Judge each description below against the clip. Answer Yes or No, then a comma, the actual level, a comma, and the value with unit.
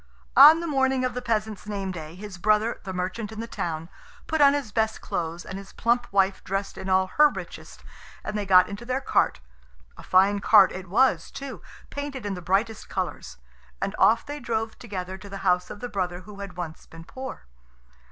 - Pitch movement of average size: Yes, average, 4.2 semitones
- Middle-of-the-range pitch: No, high, 205 Hz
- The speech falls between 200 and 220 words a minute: Yes, fast, 205 wpm